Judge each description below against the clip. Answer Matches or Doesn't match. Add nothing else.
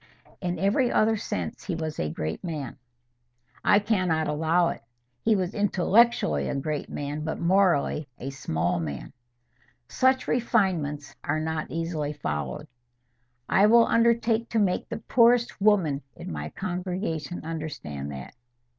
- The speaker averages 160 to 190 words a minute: Doesn't match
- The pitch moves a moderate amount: Doesn't match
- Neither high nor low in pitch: Matches